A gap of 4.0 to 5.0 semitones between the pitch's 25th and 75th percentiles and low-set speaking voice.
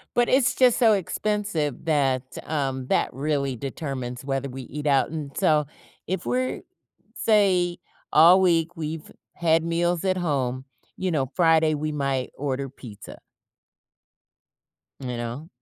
No: average, 4.6 semitones; medium, 155 Hz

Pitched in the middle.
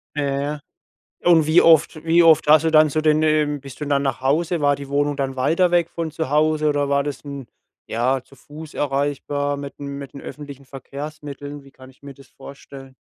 Yes: medium, 145 Hz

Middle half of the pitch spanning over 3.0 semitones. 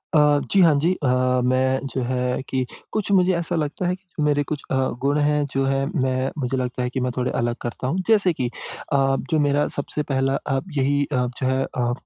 No: average, 2.7 semitones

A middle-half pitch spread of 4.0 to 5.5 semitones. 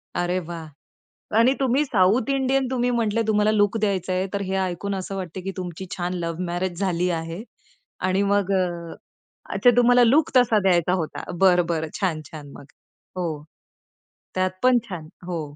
Yes: average, 4.3 semitones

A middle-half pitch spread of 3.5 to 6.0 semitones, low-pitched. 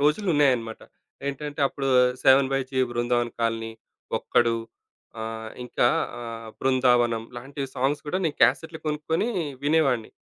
Yes: average, 3.8 semitones; low, 130 Hz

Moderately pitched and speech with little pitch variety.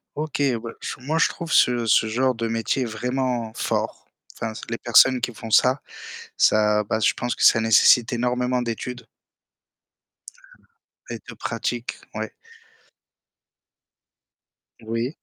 No: low, 120 Hz; narrow, 2.0 semitones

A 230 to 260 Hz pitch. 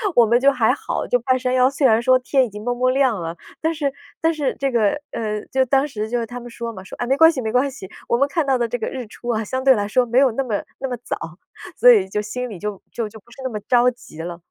Yes: high, 245 Hz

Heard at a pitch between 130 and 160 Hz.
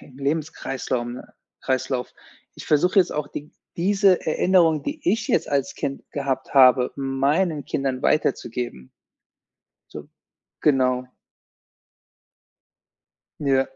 Yes: medium, 140 Hz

